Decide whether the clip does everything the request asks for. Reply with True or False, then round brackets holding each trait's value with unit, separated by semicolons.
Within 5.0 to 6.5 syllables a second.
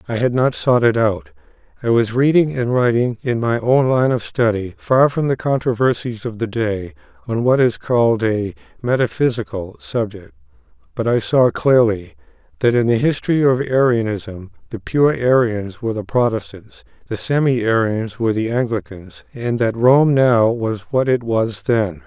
False (4.6 syllables/s)